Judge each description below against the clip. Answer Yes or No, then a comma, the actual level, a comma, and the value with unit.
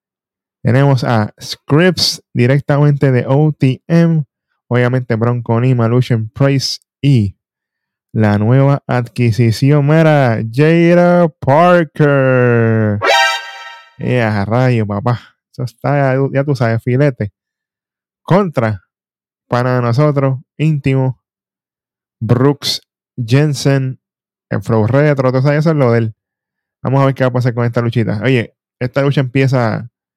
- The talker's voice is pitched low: Yes, low, 130 Hz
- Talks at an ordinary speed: No, slow, 110 wpm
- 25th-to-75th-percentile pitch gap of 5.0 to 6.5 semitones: No, average, 3.1 semitones